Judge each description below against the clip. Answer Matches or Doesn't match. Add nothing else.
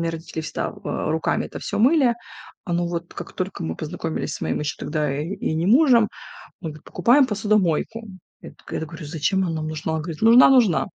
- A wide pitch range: Matches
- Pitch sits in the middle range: Matches